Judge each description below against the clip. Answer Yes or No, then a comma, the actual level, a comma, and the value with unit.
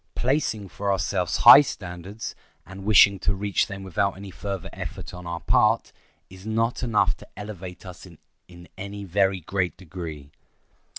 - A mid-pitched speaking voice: No, very low, 95 Hz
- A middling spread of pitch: No, narrow, 2.3 semitones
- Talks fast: No, average, 155 wpm